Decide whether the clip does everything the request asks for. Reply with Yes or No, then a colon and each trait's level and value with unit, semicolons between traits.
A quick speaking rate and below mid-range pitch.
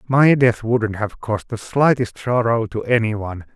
No: average, 185 wpm; low, 115 Hz